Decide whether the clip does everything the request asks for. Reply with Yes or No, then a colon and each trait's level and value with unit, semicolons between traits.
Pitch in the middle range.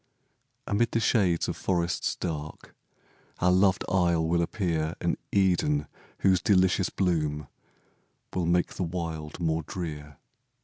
No: very low, 85 Hz